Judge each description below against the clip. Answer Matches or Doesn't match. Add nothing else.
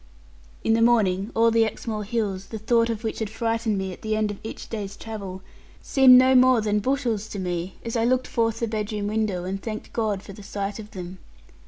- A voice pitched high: Matches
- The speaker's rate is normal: Doesn't match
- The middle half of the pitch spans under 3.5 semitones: Matches